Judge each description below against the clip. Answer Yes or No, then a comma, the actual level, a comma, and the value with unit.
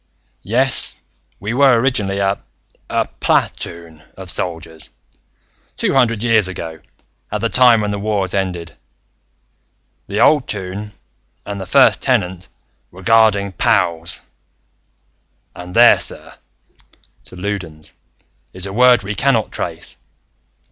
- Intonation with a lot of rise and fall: No, average, 3.9 semitones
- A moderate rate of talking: No, slow, 120 wpm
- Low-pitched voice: Yes, low, 100 Hz